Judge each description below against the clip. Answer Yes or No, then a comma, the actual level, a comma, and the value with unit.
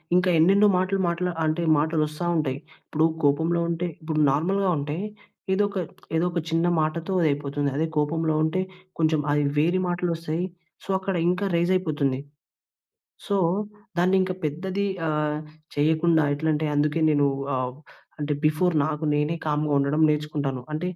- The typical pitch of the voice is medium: Yes, medium, 160 Hz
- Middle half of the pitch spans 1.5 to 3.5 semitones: Yes, average, 2.8 semitones